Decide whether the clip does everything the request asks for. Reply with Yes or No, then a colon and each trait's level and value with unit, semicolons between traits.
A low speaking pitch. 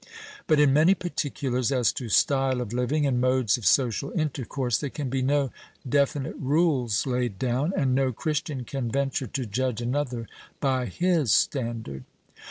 Yes: low, 130 Hz